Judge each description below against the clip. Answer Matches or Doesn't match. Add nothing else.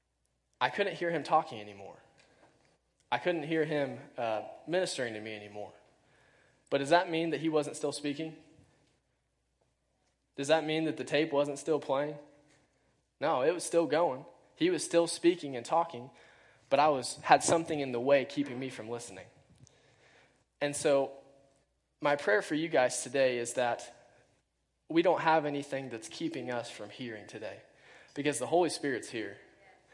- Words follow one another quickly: Doesn't match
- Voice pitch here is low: Doesn't match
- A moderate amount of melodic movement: Matches